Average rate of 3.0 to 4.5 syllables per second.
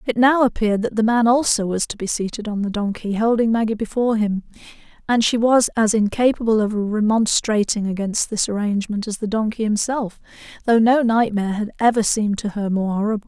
No: 5.8 syllables/s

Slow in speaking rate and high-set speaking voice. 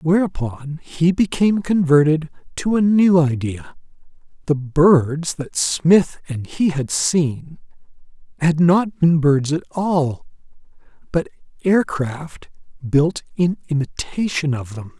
No: slow, 115 wpm; medium, 160 Hz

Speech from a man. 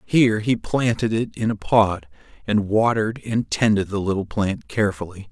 Yes: male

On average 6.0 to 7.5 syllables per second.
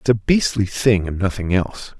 No: 5.2 syllables/s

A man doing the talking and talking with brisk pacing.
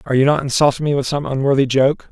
Yes: male; fast, 255 wpm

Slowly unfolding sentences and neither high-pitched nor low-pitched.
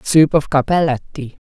Yes: slow, 120 wpm; medium, 160 Hz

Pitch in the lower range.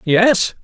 No: high, 200 Hz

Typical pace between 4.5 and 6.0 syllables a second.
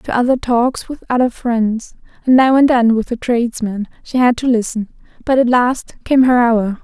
Yes: 4.8 syllables/s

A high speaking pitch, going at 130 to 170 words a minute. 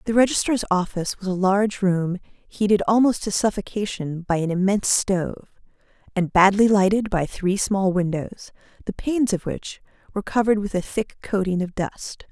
Yes: high, 195 Hz; average, 165 wpm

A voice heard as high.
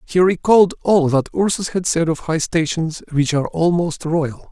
No: medium, 165 Hz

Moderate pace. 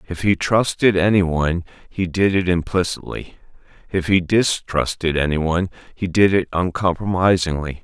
No: slow, 125 wpm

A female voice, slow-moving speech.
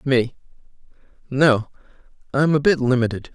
No: male; slow, 110 wpm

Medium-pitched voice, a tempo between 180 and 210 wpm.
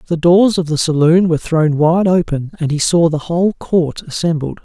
Yes: medium, 165 Hz; fast, 205 wpm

